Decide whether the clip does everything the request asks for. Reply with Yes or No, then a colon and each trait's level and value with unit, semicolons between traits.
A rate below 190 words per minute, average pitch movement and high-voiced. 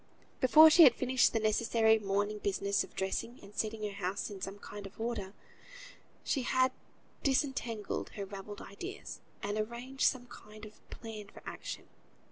Yes: average, 165 wpm; average, 3.5 semitones; high, 215 Hz